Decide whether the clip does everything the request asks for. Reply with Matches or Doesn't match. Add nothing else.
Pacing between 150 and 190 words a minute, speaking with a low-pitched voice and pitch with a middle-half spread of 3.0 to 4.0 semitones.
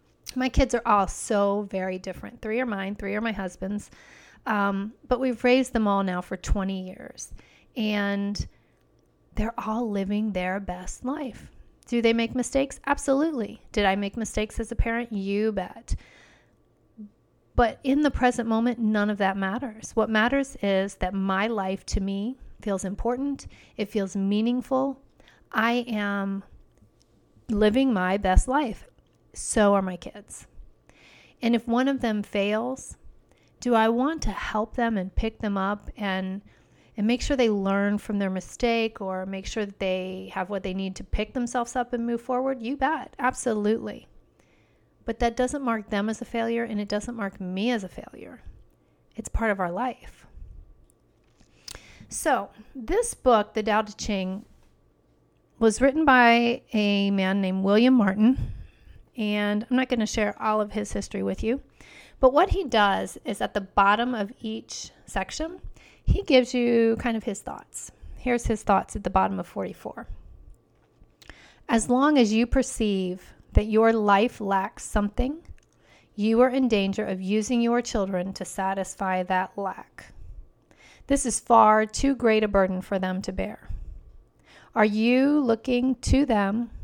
Doesn't match